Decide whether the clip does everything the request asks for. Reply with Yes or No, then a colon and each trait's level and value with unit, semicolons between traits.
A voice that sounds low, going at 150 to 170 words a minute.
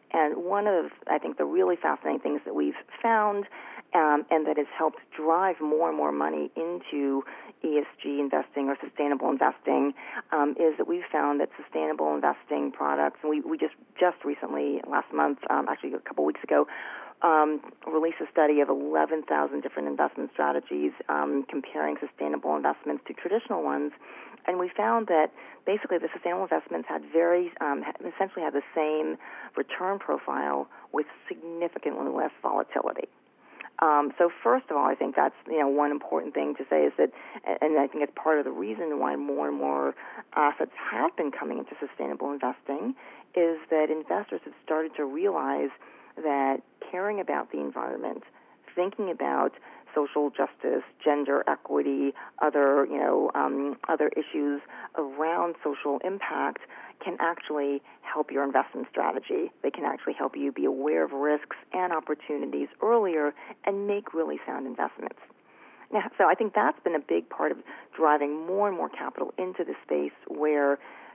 No: medium, 145 Hz; average, 165 wpm